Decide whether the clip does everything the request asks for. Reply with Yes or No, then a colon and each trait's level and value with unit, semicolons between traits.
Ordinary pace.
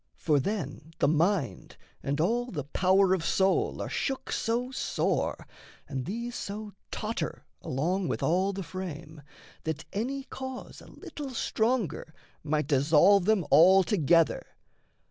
No: slow, 130 wpm